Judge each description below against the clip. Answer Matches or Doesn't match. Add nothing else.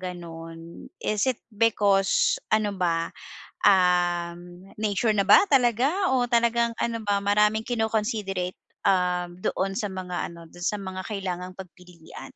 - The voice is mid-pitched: Doesn't match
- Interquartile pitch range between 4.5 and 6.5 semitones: Doesn't match